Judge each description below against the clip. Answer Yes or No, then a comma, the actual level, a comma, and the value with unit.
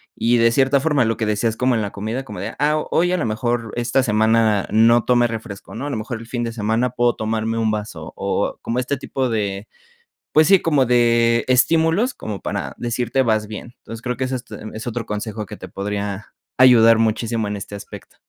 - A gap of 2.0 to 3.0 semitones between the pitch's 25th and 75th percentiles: Yes, narrow, 2.5 semitones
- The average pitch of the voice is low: Yes, low, 115 Hz